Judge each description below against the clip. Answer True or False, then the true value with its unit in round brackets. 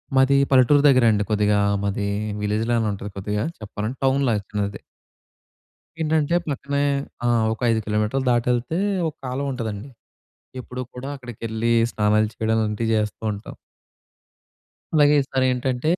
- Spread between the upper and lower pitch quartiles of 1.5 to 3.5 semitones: False (3.9 semitones)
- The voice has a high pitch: False (115 Hz)